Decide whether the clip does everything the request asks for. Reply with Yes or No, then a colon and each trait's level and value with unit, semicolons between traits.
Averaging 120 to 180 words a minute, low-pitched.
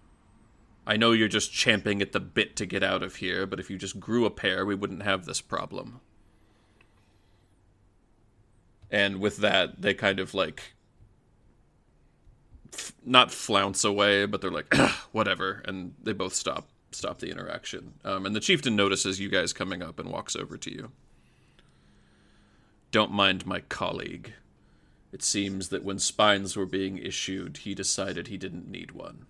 Yes: average, 160 wpm; low, 100 Hz